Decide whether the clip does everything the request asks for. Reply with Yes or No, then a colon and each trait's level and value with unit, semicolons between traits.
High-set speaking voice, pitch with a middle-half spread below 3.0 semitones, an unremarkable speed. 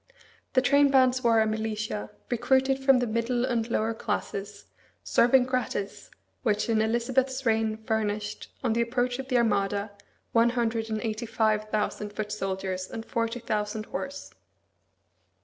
Yes: high, 225 Hz; narrow, 2.5 semitones; average, 145 wpm